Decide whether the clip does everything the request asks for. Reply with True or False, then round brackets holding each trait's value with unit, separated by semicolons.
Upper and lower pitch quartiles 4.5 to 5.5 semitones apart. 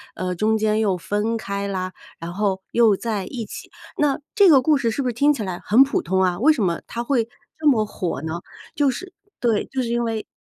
True (5.0 semitones)